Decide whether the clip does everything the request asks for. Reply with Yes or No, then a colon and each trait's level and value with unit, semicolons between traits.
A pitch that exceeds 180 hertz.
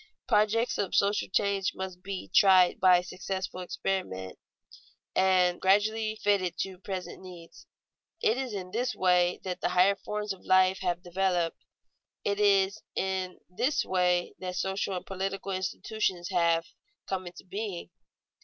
Yes: high, 190 Hz